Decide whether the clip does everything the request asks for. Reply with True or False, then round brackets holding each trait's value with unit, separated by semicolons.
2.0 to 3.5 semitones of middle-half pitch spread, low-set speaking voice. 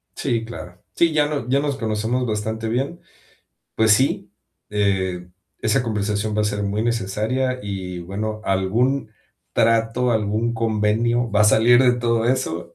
True (2.8 semitones; 110 Hz)